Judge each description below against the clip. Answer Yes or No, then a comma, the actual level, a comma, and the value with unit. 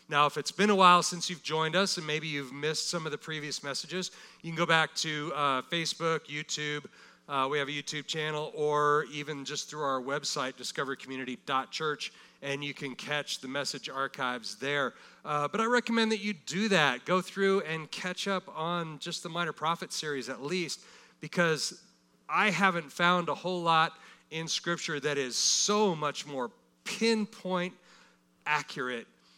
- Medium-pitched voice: Yes, medium, 155 Hz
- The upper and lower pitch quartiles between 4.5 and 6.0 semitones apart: No, average, 3.8 semitones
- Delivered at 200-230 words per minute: No, average, 175 wpm